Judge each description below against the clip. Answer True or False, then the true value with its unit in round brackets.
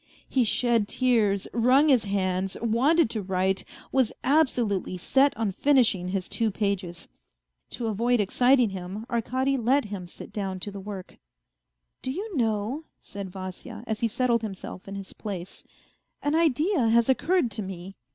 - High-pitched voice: True (220 Hz)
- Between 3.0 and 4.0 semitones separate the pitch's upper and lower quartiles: False (4.8 semitones)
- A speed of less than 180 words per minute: True (160 wpm)